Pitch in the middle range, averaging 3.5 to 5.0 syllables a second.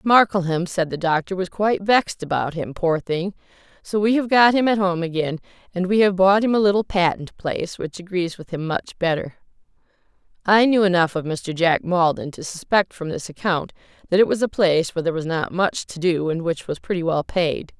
No: medium, 180 Hz; 5.5 syllables/s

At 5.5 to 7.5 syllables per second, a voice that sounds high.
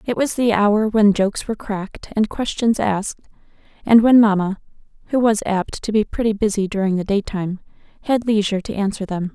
Yes: 5.7 syllables/s; high, 210 Hz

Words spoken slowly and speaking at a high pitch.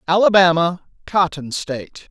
No: slow, 85 wpm; medium, 170 Hz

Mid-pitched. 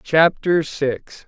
Yes: medium, 155 Hz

